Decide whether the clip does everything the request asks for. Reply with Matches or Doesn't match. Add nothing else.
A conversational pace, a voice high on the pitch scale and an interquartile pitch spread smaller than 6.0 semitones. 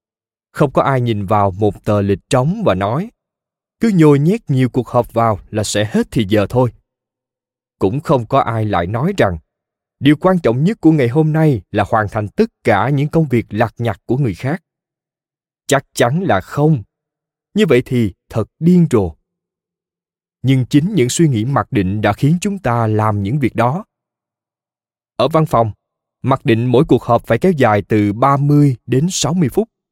Doesn't match